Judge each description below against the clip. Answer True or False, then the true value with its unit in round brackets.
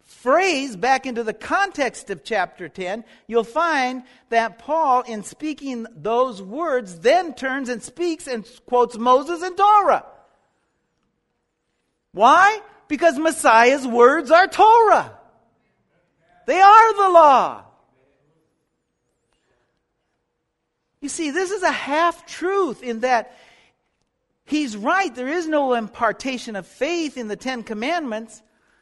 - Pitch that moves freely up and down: True (6.5 semitones)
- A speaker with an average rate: False (115 wpm)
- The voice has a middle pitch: False (260 Hz)